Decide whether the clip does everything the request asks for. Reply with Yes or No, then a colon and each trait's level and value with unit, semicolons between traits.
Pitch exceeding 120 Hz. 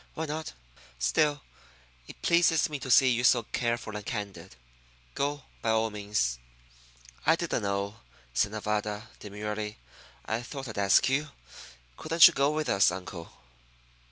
No: low, 110 Hz